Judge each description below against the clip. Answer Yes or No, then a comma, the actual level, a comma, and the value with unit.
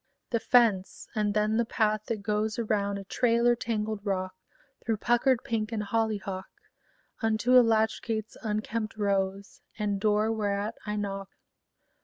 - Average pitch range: No, narrow, 2.0 semitones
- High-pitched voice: Yes, high, 215 Hz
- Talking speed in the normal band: Yes, average, 145 wpm